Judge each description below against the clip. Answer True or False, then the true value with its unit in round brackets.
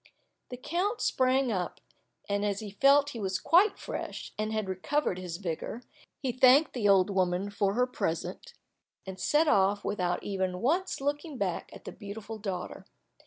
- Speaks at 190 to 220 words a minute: False (170 wpm)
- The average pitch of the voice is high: True (210 Hz)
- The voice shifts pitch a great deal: True (6.2 semitones)